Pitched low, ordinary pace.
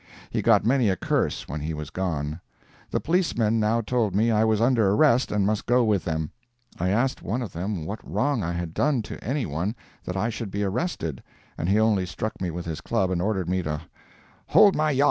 No: low, 105 Hz; fast, 220 wpm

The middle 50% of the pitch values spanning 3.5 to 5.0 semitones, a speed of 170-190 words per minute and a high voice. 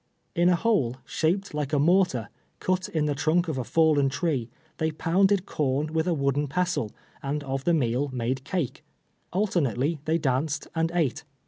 No: average, 4.1 semitones; average, 175 wpm; medium, 155 Hz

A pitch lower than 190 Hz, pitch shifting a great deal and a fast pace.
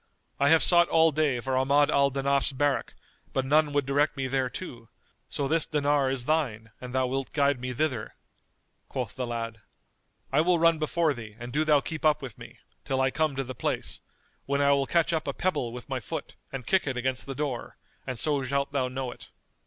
No: medium, 140 Hz; average, 2.8 semitones; fast, 215 wpm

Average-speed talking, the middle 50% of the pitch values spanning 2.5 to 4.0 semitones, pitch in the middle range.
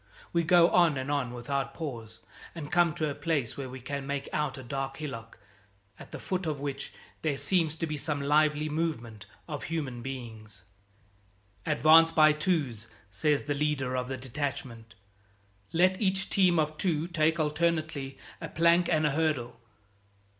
Yes: average, 165 wpm; average, 3.5 semitones; medium, 150 Hz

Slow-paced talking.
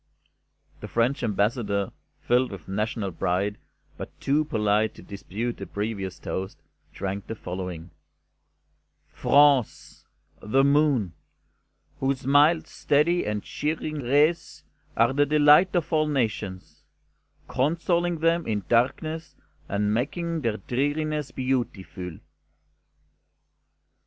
Yes: slow, 105 wpm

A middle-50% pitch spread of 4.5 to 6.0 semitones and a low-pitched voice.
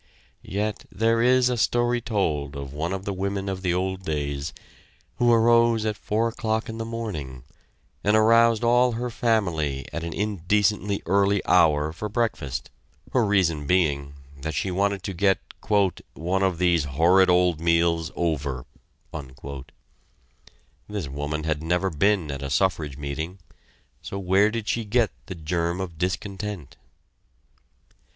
Yes: average, 5.1 semitones; very low, 95 Hz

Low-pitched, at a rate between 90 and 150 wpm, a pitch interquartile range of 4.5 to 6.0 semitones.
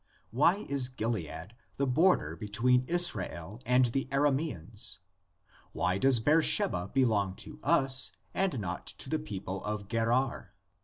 Yes: low, 120 Hz; slow, 135 wpm; wide, 5.5 semitones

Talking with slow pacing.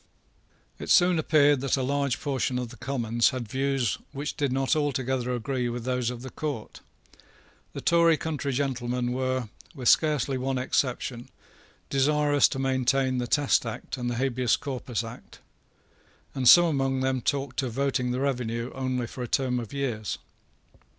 No: average, 165 wpm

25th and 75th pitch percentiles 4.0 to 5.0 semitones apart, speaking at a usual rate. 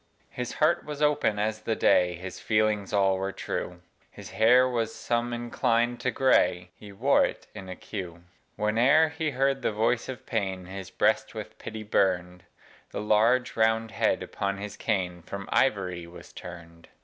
Yes: average, 4.3 semitones; average, 170 wpm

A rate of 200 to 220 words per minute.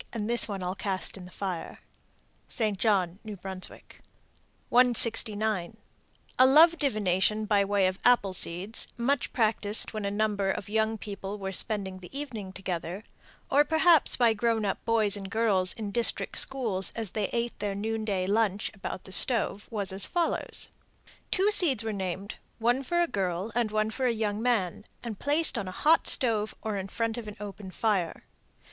No: average, 175 wpm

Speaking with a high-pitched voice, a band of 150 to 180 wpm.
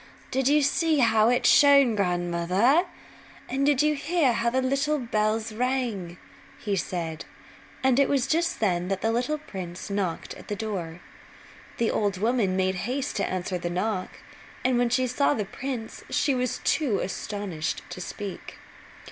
Yes: high, 225 Hz; average, 165 wpm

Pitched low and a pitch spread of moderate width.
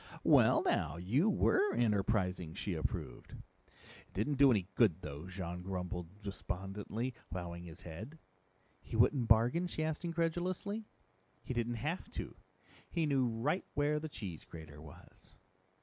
No: low, 110 Hz; wide, 8.7 semitones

